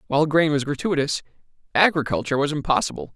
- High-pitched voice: No, medium, 150 Hz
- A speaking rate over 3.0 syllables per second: Yes, 6.9 syllables/s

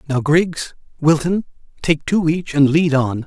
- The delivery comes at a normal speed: Yes, average, 145 wpm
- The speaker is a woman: No, male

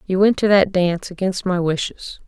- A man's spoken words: No, female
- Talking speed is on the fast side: Yes, fast, 210 wpm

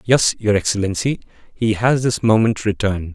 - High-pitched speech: No, low, 110 Hz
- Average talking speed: Yes, average, 150 wpm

